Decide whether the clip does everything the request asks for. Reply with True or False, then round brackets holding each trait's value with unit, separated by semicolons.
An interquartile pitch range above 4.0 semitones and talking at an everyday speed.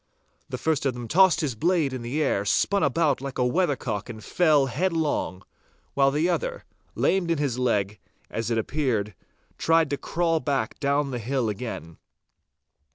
True (5.4 semitones; 165 wpm)